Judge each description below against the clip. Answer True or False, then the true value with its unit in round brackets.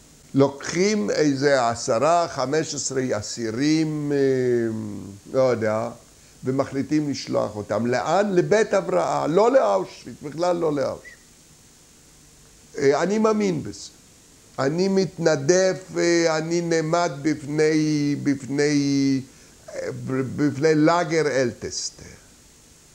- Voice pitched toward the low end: False (145 Hz)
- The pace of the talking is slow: True (90 wpm)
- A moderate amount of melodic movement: True (4.2 semitones)